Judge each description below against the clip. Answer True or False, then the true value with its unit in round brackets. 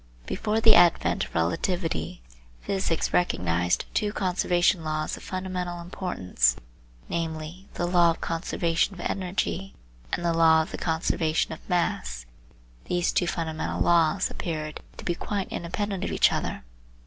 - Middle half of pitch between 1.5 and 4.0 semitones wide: True (2.5 semitones)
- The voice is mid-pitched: True (170 Hz)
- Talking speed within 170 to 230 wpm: False (145 wpm)